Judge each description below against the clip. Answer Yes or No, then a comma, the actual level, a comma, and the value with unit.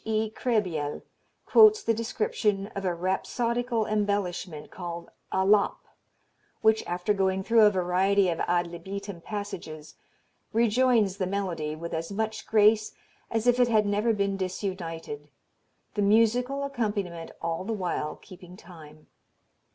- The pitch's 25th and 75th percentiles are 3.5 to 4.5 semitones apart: Yes, average, 3.8 semitones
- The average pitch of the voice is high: Yes, high, 200 Hz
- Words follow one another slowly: Yes, slow, 130 wpm